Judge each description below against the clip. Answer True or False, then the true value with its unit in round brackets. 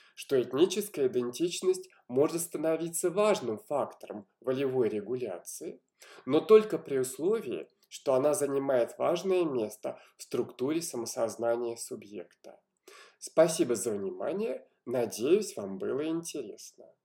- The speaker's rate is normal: False (100 wpm)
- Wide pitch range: True (8.6 semitones)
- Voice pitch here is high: False (170 Hz)